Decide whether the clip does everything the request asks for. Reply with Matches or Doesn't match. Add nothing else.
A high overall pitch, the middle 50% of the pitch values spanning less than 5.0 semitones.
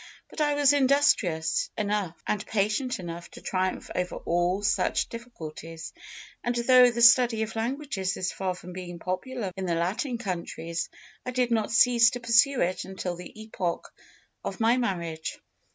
Doesn't match